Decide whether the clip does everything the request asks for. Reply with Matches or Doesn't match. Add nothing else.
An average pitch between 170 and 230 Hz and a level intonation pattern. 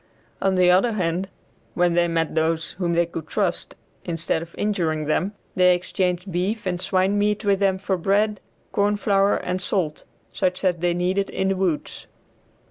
Matches